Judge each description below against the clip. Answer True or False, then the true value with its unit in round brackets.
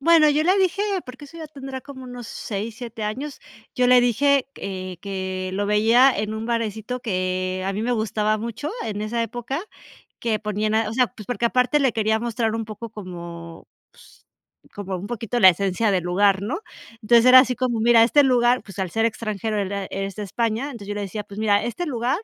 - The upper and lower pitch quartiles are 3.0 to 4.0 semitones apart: True (3.6 semitones)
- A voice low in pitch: False (225 Hz)